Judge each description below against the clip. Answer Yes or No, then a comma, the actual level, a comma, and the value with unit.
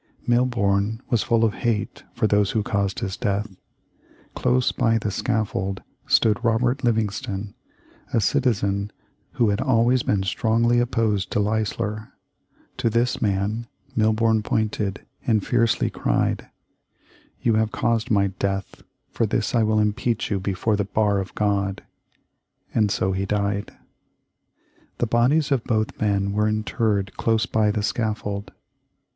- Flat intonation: Yes, narrow, 2.3 semitones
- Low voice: Yes, low, 110 Hz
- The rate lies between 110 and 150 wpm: Yes, average, 140 wpm